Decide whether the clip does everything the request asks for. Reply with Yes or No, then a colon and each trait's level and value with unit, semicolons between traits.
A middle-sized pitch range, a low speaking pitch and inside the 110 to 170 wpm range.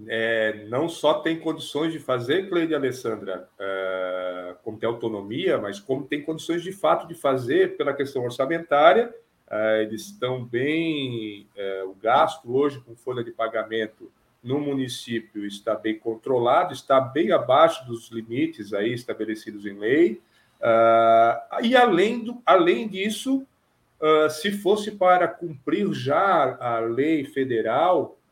No: wide, 6.6 semitones; low, 130 Hz; average, 140 wpm